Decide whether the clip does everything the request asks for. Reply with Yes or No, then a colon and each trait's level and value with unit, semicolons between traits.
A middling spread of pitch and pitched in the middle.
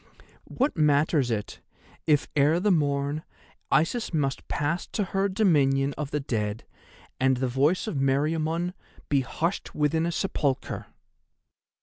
Yes: average, 3.7 semitones; medium, 150 Hz